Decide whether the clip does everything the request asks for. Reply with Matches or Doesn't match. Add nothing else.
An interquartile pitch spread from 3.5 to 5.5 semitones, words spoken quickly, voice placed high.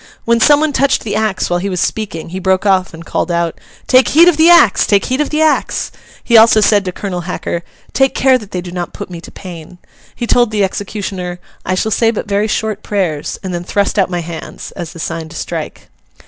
Matches